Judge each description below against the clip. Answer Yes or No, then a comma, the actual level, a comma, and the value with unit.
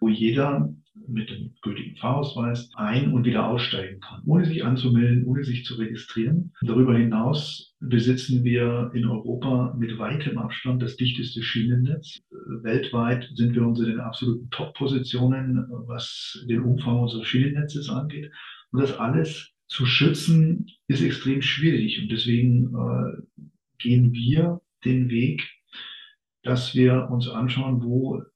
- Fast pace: No, average, 135 wpm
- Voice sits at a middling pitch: No, low, 125 Hz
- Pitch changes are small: Yes, narrow, 2.3 semitones